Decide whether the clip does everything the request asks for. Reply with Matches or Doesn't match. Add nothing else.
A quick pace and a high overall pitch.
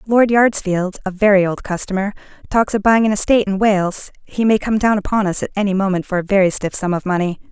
Matches